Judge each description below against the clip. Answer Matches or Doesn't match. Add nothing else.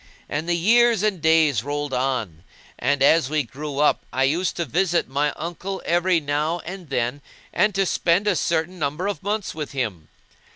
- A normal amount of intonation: Matches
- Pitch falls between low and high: Matches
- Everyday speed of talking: Matches